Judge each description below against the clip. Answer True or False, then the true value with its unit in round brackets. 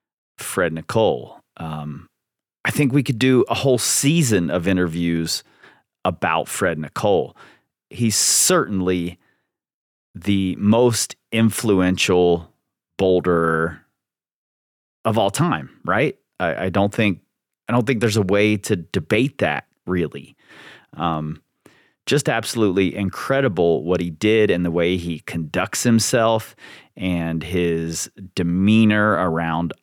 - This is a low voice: True (95 Hz)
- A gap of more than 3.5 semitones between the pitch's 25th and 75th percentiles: True (4.7 semitones)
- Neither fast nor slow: False (115 wpm)